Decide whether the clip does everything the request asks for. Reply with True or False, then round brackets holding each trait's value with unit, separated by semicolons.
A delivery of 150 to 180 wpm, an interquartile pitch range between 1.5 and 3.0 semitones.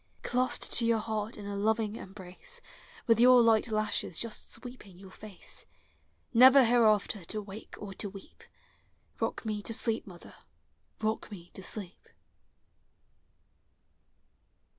False (140 wpm; 2.5 semitones)